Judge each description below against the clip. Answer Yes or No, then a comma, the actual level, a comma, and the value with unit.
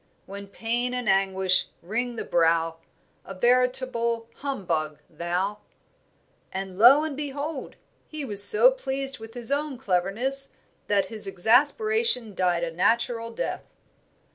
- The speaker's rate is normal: No, slow, 125 wpm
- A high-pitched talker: Yes, high, 230 Hz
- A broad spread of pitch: Yes, wide, 5.7 semitones